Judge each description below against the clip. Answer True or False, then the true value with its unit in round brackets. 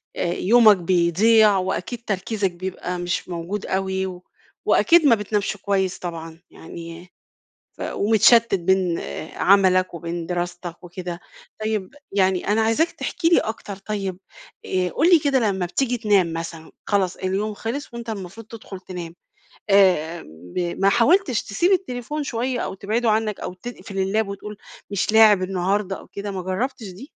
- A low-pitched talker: False (195 Hz)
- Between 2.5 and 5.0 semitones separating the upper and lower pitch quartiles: True (3.5 semitones)